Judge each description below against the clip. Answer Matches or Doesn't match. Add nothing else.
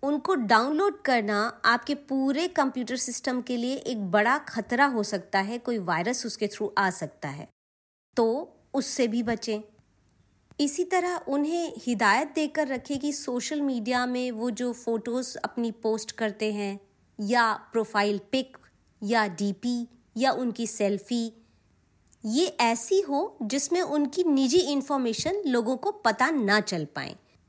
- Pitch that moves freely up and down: Doesn't match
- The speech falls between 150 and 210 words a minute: Doesn't match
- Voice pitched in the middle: Doesn't match